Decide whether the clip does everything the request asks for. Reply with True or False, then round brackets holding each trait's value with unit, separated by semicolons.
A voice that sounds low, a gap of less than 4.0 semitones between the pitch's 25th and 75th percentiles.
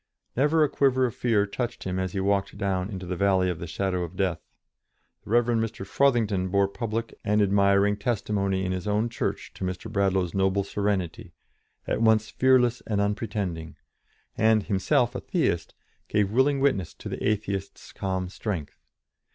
True (100 Hz; 3.2 semitones)